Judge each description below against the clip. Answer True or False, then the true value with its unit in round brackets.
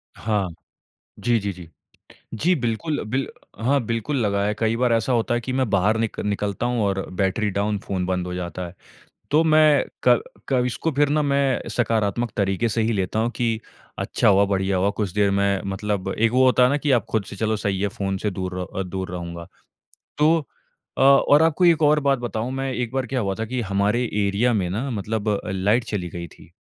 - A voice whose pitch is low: True (110 Hz)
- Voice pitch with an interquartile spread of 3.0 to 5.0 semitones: True (4.3 semitones)